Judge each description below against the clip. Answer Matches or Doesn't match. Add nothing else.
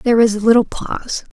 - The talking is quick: Matches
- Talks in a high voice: Matches